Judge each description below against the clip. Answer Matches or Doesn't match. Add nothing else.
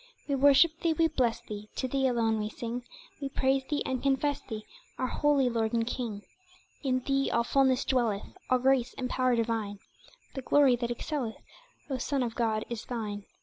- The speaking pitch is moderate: Doesn't match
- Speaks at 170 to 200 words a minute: Matches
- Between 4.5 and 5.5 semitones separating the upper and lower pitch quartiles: Doesn't match